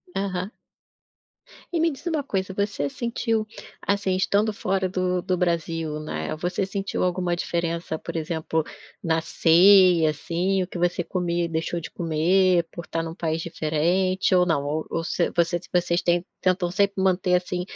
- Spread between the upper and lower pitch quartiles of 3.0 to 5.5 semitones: No, narrow, 2.4 semitones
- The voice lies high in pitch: No, medium, 180 Hz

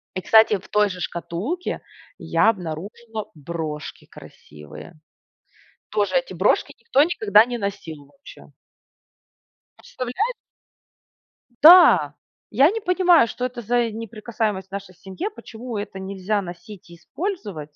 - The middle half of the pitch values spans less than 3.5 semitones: No, average, 5.1 semitones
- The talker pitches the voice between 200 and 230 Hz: Yes, high, 210 Hz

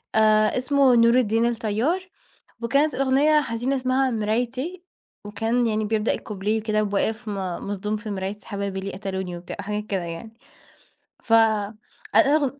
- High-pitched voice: Yes, high, 220 Hz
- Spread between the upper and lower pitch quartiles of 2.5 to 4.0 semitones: Yes, average, 3.5 semitones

